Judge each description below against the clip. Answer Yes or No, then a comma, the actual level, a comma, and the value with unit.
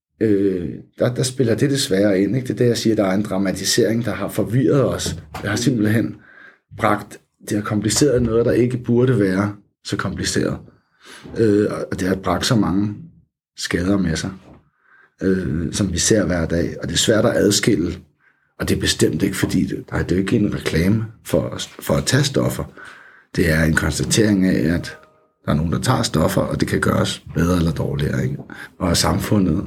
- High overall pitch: No, low, 100 Hz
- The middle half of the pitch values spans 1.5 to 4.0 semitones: Yes, average, 3.5 semitones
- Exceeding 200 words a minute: No, average, 195 wpm